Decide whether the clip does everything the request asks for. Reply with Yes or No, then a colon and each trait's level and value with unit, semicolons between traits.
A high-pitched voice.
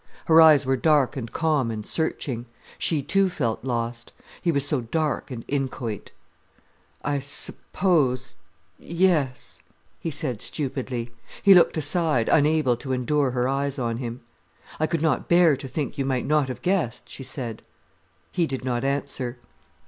No: low, 135 Hz